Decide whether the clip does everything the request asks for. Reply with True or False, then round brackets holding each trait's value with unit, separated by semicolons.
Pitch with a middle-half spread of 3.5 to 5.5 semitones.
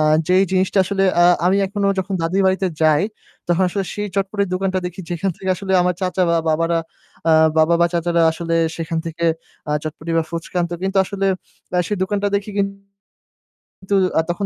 False (2.7 semitones)